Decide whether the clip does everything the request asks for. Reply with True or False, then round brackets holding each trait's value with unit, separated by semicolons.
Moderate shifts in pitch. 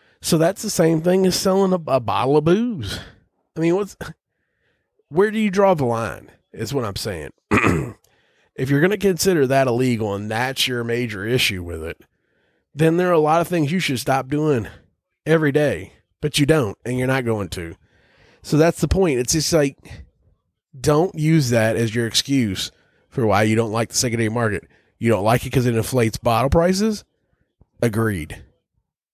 False (6.5 semitones)